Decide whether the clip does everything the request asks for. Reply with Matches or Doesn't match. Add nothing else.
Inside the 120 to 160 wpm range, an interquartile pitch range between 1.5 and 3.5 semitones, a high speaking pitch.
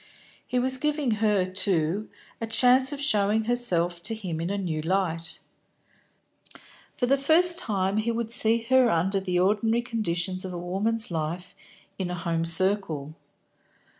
Doesn't match